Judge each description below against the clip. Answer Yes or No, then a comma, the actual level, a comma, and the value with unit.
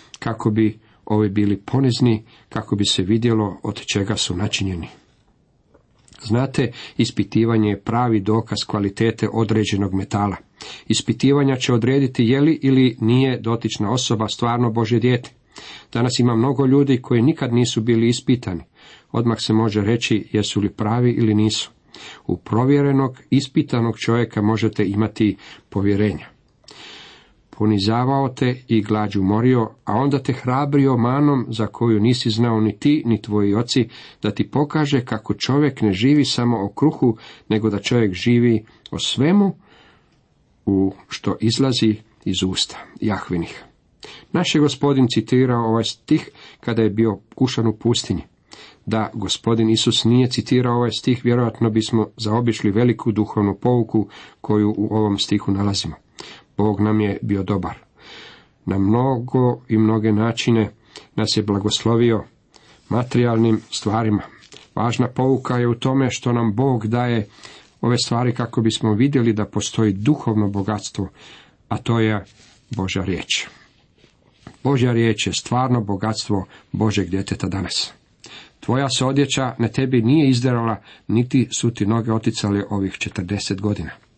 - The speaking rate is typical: Yes, average, 135 wpm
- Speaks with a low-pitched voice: Yes, low, 115 Hz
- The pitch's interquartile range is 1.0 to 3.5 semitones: Yes, average, 2.8 semitones